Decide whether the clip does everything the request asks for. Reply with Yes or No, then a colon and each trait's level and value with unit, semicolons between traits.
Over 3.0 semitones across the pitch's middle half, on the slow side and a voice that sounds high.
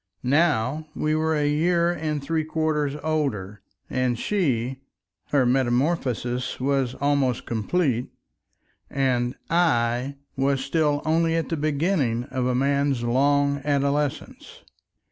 No: average, 3.6 semitones; slow, 110 wpm; medium, 140 Hz